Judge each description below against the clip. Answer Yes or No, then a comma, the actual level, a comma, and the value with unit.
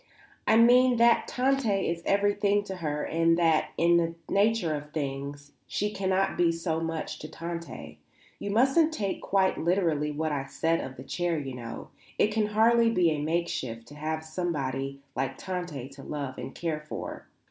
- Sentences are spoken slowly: No, average, 175 wpm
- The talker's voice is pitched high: No, medium, 170 Hz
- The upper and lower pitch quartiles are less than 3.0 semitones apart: No, average, 5.2 semitones